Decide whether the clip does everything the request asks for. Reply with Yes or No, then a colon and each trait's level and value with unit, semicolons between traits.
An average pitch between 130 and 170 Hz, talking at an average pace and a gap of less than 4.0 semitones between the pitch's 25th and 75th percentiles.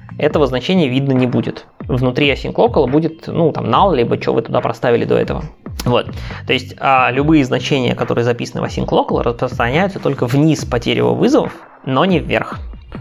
No: medium, 140 Hz; fast, 180 wpm; average, 3.4 semitones